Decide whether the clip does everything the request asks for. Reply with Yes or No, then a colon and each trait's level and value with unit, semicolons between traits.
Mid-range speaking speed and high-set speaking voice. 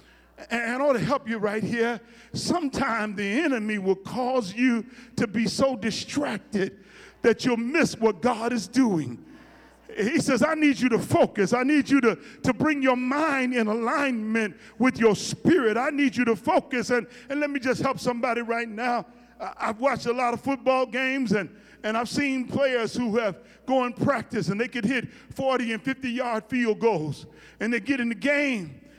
Yes: average, 190 wpm; high, 240 Hz